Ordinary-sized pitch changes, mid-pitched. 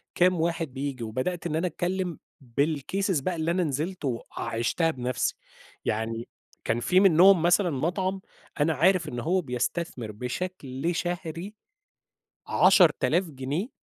No: wide, 5.7 semitones; medium, 165 Hz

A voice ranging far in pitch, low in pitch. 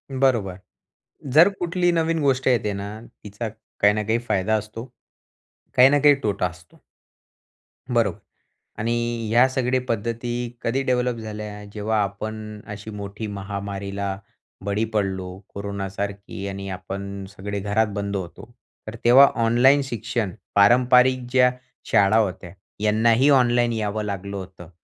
No: average, 3.4 semitones; low, 105 Hz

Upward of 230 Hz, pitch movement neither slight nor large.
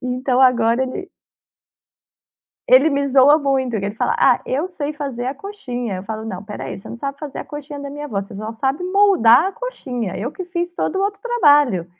Yes: very high, 270 Hz; average, 4.7 semitones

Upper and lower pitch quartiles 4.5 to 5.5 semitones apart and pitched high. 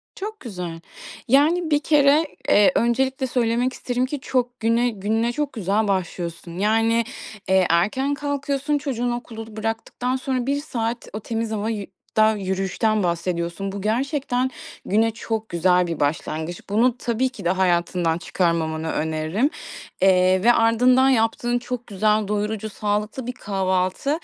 Yes: average, 5.0 semitones; high, 225 Hz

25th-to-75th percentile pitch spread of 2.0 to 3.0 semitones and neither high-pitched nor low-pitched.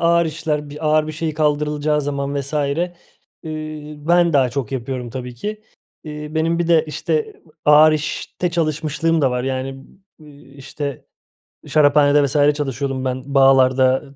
Yes: narrow, 2.4 semitones; medium, 145 Hz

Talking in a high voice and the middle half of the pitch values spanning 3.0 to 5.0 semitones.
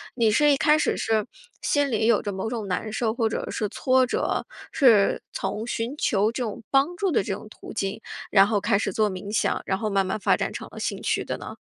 Yes: high, 220 Hz; average, 3.8 semitones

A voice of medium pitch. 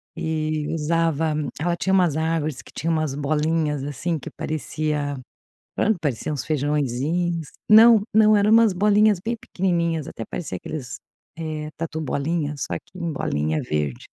Yes: medium, 155 Hz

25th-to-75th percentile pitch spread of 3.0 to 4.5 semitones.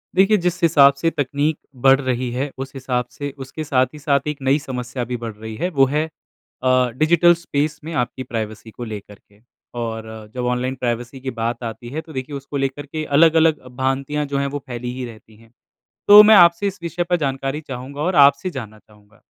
Yes: average, 3.8 semitones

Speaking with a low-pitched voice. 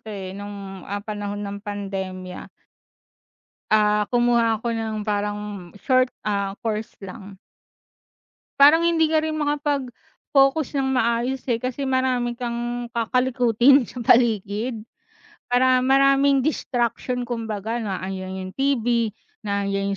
No: high, 235 Hz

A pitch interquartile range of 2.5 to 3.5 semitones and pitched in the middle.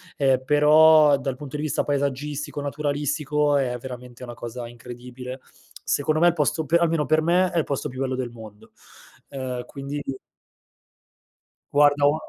Yes: average, 2.8 semitones; medium, 145 Hz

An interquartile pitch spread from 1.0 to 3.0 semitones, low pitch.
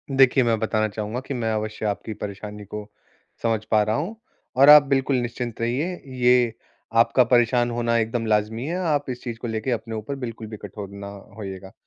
Yes: average, 2.7 semitones; low, 115 Hz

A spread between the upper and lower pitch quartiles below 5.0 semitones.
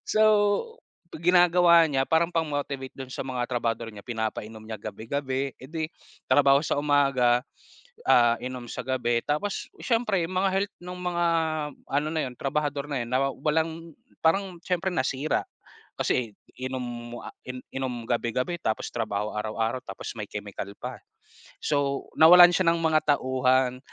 No: average, 5.3 semitones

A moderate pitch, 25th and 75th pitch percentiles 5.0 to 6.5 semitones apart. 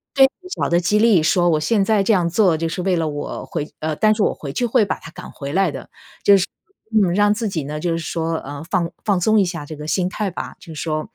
No: medium, 175 Hz; average, 4.6 semitones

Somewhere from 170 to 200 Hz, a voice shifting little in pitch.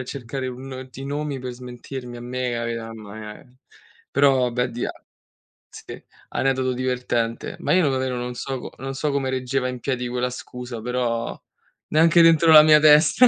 No: low, 130 Hz; narrow, 1.9 semitones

